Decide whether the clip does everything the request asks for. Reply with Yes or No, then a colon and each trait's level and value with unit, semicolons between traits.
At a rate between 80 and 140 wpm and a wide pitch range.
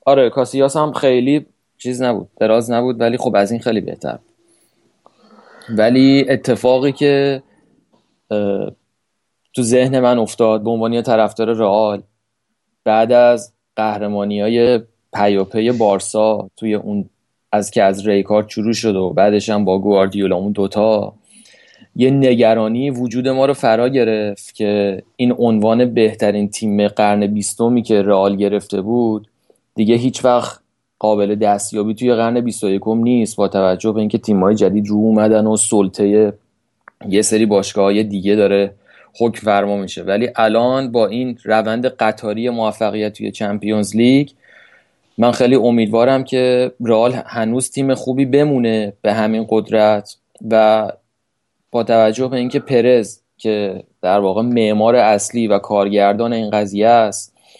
No: average, 135 wpm; average, 2.7 semitones